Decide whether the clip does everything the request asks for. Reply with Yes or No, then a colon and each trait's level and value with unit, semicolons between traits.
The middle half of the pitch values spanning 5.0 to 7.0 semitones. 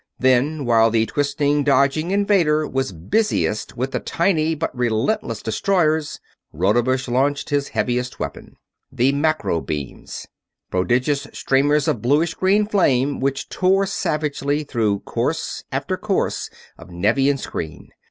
No: average, 4.4 semitones